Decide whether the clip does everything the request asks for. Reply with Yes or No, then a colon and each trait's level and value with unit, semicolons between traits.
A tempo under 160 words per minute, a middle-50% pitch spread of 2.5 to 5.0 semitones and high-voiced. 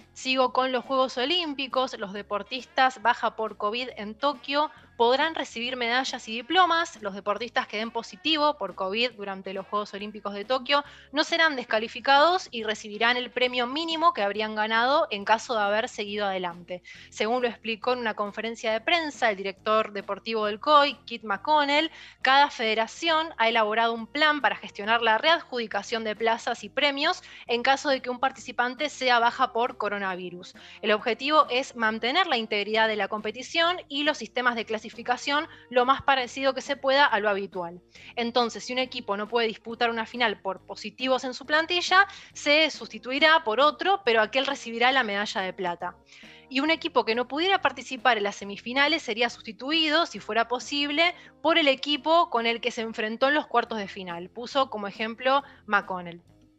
No: average, 175 wpm; average, 4.4 semitones; high, 240 Hz